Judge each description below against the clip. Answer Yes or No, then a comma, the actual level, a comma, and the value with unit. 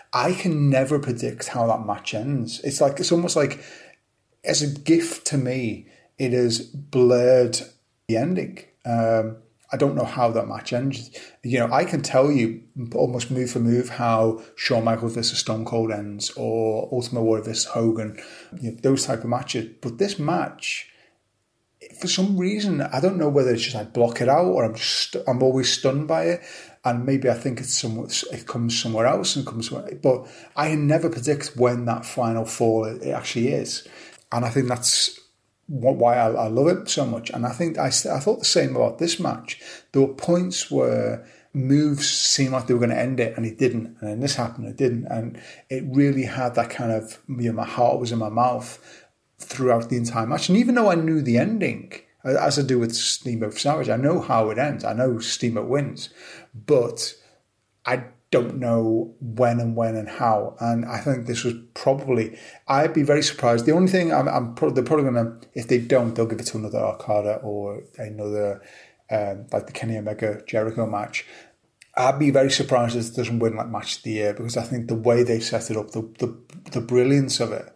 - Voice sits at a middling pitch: No, low, 120 Hz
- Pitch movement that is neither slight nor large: Yes, average, 3.1 semitones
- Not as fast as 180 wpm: No, fast, 205 wpm